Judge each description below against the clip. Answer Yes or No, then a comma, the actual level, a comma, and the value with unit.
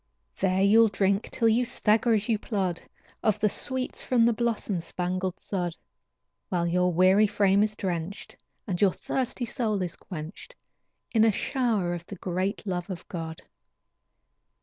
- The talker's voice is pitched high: Yes, high, 200 Hz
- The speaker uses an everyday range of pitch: Yes, average, 3.7 semitones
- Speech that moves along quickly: No, average, 155 wpm